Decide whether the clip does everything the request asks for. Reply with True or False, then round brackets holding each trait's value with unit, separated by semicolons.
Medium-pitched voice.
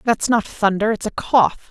False (215 Hz)